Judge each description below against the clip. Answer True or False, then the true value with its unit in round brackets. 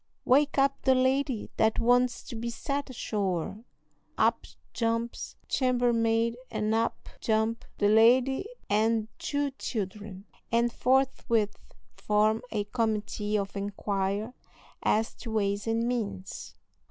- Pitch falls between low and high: False (225 Hz)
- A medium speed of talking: False (115 wpm)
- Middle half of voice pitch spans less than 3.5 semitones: True (2.9 semitones)